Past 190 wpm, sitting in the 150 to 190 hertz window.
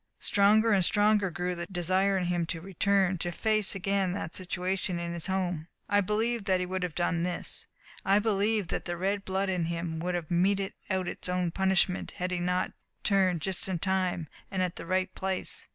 Yes: average, 200 wpm; medium, 185 Hz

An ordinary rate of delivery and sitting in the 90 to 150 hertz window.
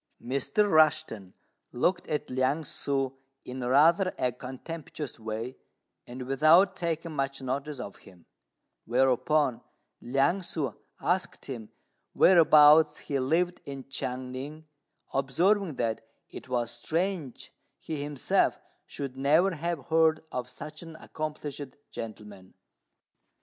No: slow, 115 wpm; medium, 140 Hz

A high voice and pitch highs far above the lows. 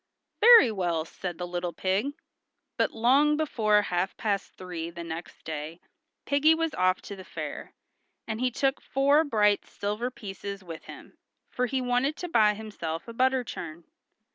Yes: high, 210 Hz; wide, 6.6 semitones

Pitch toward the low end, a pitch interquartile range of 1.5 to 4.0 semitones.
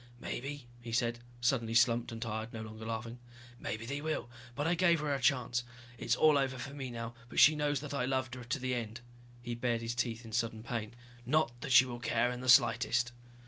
Yes: low, 120 Hz; average, 2.7 semitones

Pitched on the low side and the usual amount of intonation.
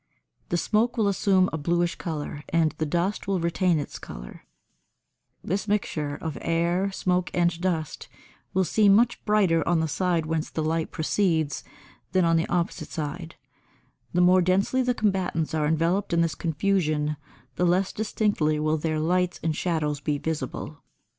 No: medium, 170 Hz; average, 3.0 semitones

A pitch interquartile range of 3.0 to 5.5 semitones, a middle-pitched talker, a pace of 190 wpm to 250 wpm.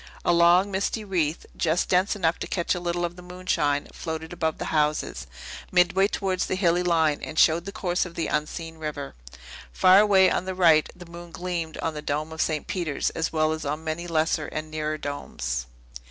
No: narrow, 2.5 semitones; medium, 165 Hz; average, 200 wpm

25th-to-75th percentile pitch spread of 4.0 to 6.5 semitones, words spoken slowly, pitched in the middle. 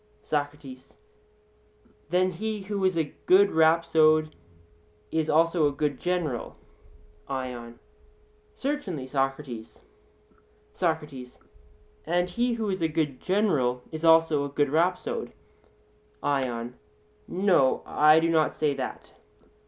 Yes: average, 4.3 semitones; slow, 110 wpm; medium, 155 Hz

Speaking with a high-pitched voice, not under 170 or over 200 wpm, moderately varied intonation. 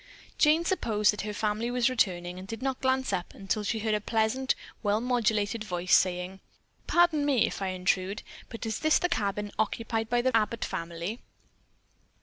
Yes: high, 220 Hz; average, 175 wpm; average, 3.8 semitones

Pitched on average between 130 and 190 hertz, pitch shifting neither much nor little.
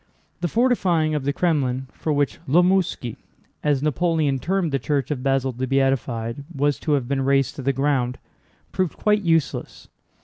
Yes: medium, 140 Hz; average, 3.7 semitones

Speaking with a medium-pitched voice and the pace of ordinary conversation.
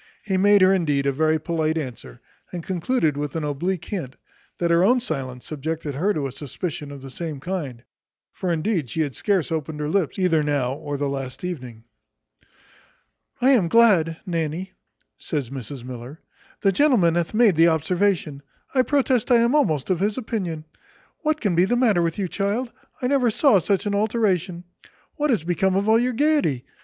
Yes: medium, 170 Hz; average, 185 wpm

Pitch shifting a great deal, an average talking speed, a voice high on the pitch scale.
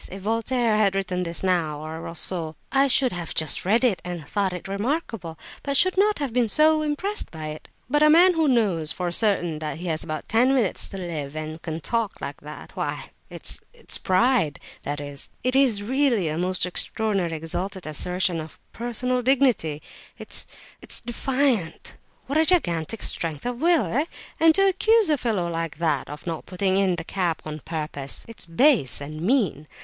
Yes: wide, 7.8 semitones; average, 180 wpm; high, 195 Hz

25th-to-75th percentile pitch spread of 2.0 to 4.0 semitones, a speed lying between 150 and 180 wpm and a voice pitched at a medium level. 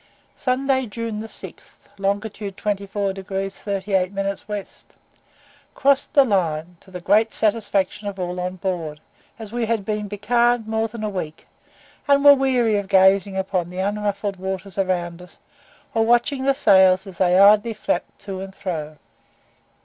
No: average, 2.8 semitones; average, 155 wpm; high, 200 Hz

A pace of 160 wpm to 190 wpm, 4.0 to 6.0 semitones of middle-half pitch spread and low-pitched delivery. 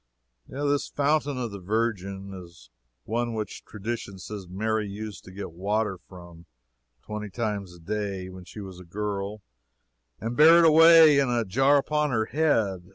Yes: average, 165 wpm; average, 4.4 semitones; low, 105 Hz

